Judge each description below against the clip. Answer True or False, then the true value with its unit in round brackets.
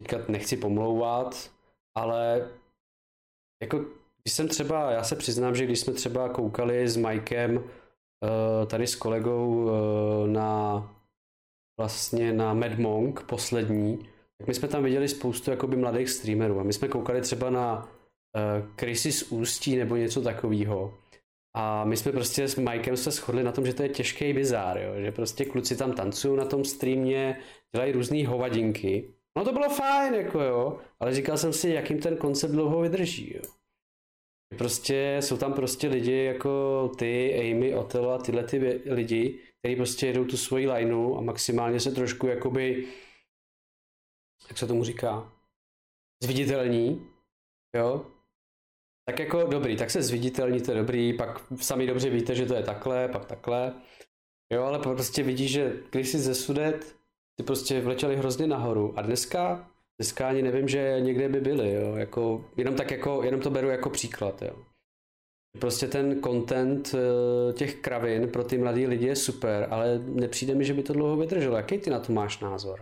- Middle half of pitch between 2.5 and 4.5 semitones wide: True (2.9 semitones)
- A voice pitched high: False (125 Hz)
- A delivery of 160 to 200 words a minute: True (165 wpm)